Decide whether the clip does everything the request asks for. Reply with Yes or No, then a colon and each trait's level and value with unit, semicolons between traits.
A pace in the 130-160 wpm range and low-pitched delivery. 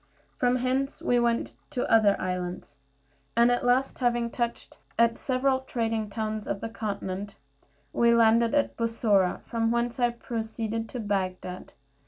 No: average, 145 wpm; high, 230 Hz